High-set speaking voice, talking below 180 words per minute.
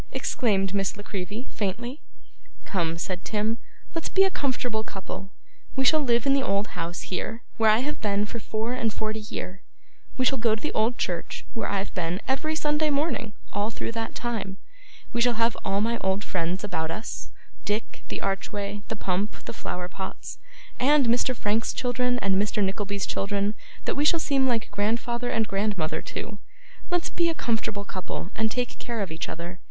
No: high, 215 Hz; average, 185 wpm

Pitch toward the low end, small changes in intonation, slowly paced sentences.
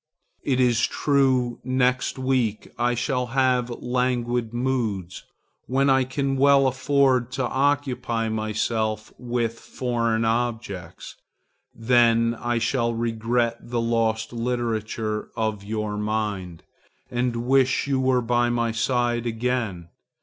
Yes: low, 120 Hz; narrow, 2.3 semitones; slow, 115 wpm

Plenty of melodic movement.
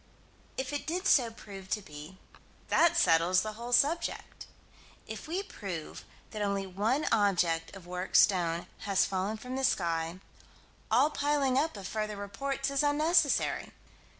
Yes: wide, 6.9 semitones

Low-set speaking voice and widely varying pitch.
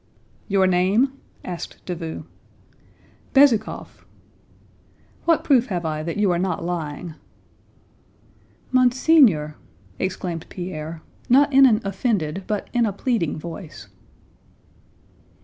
No: medium, 185 Hz; wide, 6.4 semitones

